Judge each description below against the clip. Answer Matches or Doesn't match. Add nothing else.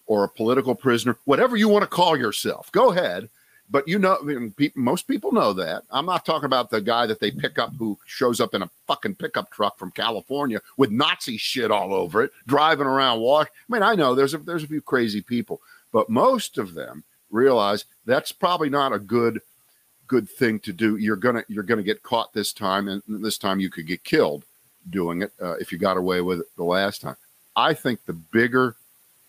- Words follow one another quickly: Matches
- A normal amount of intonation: Doesn't match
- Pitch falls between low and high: Doesn't match